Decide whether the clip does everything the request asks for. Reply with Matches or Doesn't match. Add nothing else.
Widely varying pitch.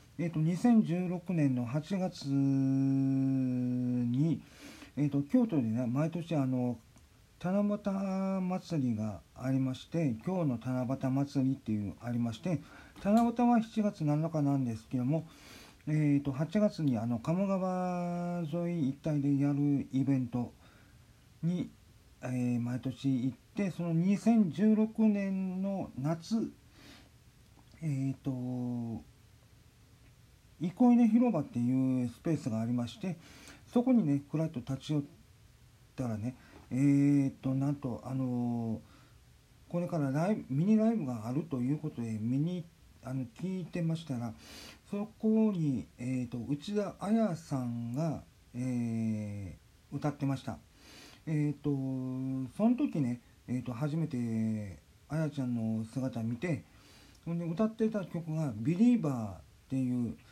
Matches